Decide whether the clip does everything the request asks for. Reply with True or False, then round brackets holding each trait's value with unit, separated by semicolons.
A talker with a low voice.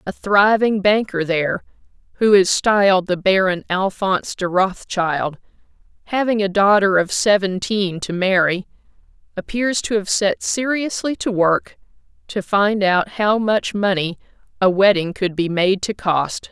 False (195 Hz)